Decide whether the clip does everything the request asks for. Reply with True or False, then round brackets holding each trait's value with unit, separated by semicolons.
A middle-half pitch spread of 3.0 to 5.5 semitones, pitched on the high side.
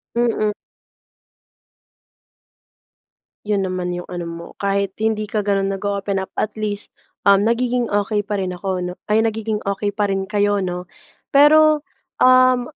False (2.4 semitones; 205 Hz)